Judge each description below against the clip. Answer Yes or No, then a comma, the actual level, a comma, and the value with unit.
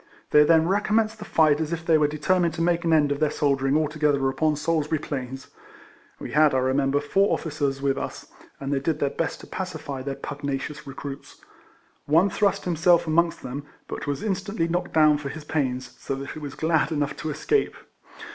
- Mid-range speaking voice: Yes, medium, 150 Hz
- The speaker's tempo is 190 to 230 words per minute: Yes, average, 200 wpm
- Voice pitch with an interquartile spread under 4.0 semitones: Yes, average, 2.8 semitones